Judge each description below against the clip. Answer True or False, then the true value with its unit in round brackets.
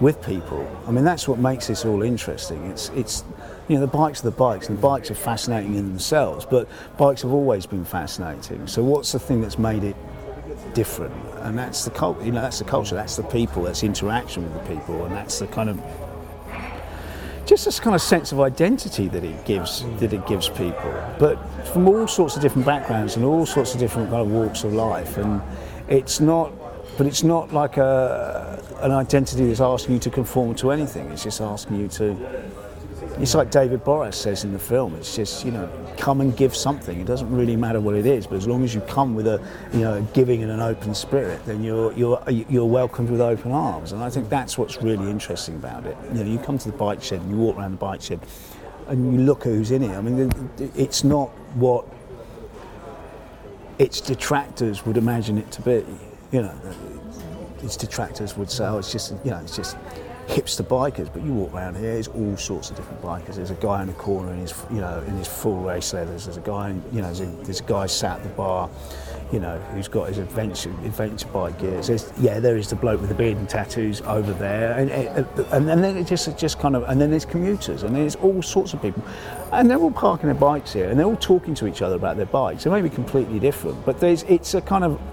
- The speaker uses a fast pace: True (235 wpm)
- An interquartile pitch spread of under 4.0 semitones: False (5.1 semitones)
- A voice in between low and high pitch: False (115 Hz)